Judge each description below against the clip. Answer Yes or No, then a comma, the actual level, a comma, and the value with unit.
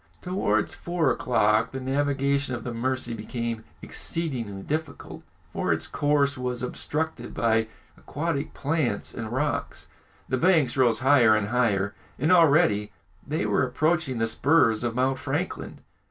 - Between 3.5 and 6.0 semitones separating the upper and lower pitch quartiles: Yes, average, 4.1 semitones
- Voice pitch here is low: Yes, low, 130 Hz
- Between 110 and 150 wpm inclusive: Yes, average, 140 wpm